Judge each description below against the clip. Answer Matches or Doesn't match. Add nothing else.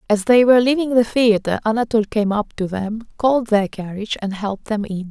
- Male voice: Doesn't match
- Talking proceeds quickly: Matches